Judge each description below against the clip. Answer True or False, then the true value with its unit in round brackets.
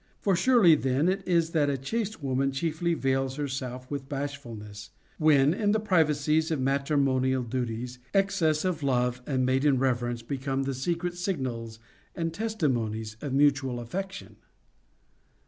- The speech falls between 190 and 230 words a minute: False (140 wpm)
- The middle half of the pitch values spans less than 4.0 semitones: False (4.3 semitones)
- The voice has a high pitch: False (140 Hz)